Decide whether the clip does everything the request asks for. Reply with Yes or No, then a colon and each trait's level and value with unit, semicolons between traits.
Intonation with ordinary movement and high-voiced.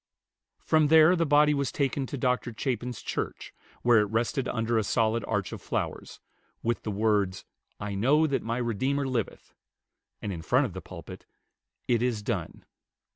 No: average, 4.5 semitones; low, 120 Hz